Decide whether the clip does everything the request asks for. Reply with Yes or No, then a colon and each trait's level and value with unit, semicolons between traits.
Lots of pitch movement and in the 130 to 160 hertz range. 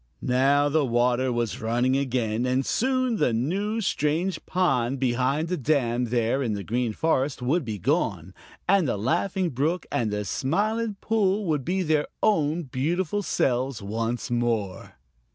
Yes: wide, 6.6 semitones; low, 135 Hz